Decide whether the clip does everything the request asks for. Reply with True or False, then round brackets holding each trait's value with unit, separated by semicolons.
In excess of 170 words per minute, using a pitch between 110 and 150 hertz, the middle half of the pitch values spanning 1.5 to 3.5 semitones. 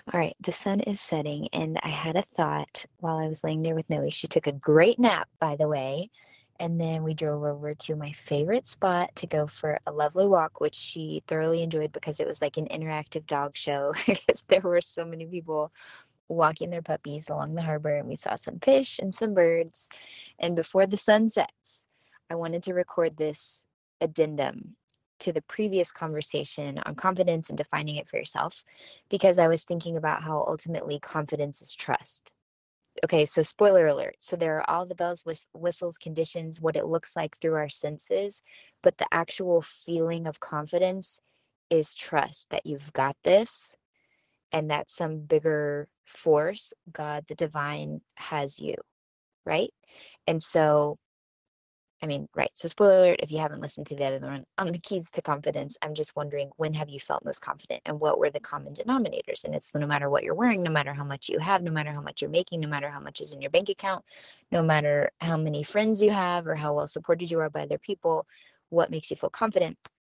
False (200 wpm; 160 Hz; 2.8 semitones)